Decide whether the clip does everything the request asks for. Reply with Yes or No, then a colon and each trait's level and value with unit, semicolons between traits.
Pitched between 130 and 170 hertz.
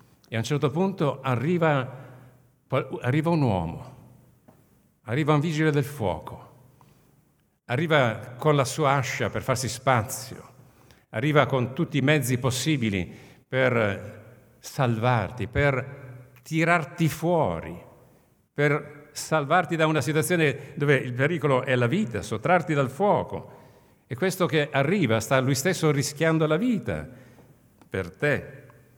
Yes: medium, 140 Hz